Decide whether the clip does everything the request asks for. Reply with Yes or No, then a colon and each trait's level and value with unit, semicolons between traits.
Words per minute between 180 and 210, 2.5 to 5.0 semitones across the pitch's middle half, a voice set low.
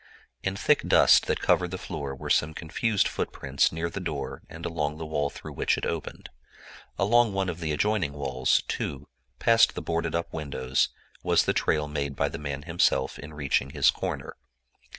Yes: average, 185 wpm; average, 3.2 semitones; very low, 80 Hz